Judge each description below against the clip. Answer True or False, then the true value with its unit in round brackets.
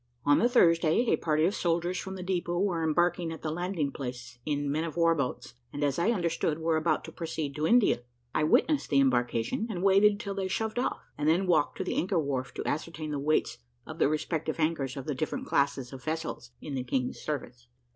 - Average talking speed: False (220 wpm)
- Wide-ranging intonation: False (3.9 semitones)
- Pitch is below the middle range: False (160 Hz)